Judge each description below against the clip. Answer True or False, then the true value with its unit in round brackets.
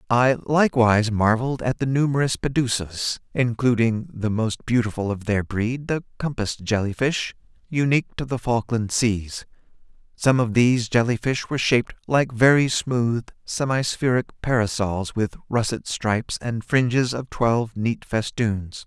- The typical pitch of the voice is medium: False (120 Hz)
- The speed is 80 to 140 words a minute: True (135 wpm)